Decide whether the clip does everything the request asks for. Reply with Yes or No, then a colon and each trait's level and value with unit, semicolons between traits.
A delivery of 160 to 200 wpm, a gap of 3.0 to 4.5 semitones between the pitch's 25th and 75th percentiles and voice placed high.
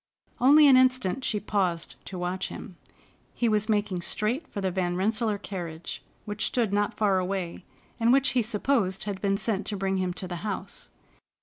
Yes: average, 185 wpm; average, 3.3 semitones; high, 205 Hz